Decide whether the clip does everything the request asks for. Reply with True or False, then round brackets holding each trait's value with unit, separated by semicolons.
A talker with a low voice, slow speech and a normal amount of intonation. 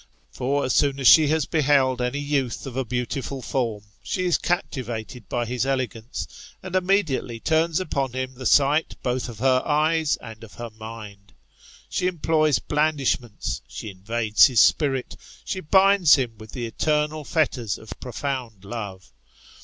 False (130 Hz; 160 wpm; 4.5 semitones)